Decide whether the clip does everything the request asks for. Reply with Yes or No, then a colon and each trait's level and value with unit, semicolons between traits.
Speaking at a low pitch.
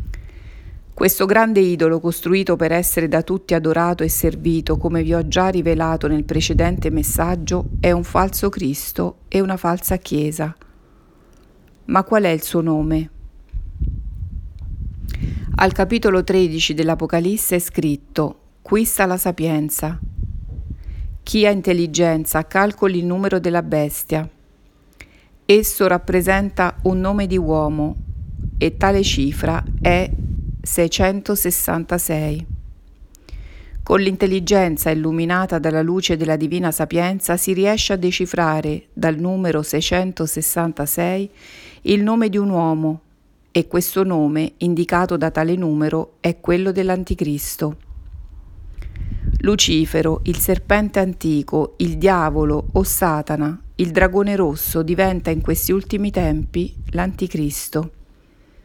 No: medium, 165 Hz